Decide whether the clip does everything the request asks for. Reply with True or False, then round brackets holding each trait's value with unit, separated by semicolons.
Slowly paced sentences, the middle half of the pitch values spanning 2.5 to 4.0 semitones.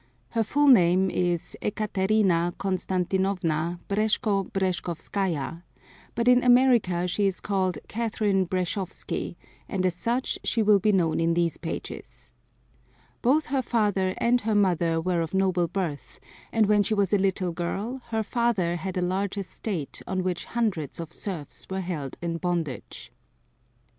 False (145 wpm; 3.5 semitones)